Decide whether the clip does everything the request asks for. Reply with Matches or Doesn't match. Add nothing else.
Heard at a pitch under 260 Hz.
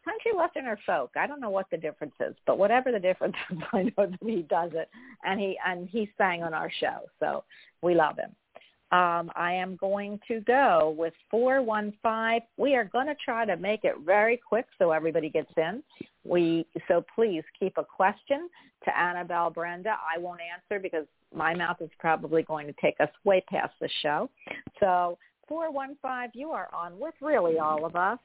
Matches